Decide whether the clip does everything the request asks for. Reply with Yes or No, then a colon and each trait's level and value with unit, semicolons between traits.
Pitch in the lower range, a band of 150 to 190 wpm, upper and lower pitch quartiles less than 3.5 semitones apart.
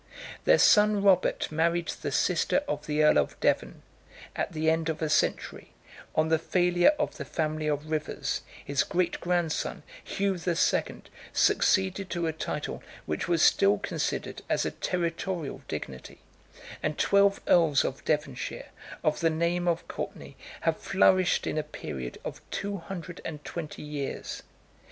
No: medium, 165 Hz; average, 155 wpm; average, 2.8 semitones